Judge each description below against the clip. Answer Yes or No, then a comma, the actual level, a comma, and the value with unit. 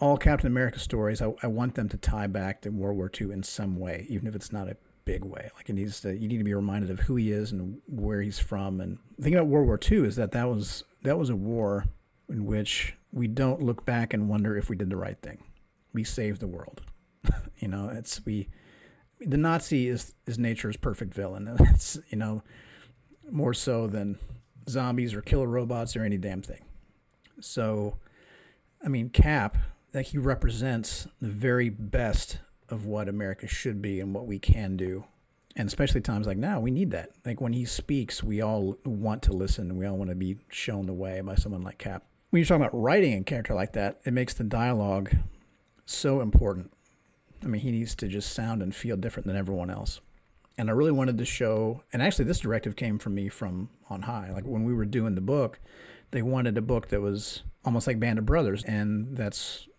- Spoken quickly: Yes, fast, 215 wpm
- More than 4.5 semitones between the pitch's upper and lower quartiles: No, average, 3.6 semitones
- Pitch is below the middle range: Yes, low, 105 Hz